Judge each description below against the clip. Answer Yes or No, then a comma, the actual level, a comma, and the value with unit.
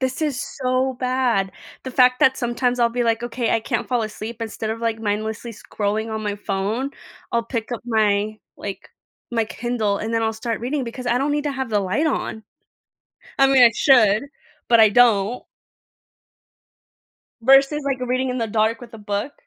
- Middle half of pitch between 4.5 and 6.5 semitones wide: No, average, 2.7 semitones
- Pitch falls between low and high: No, high, 235 Hz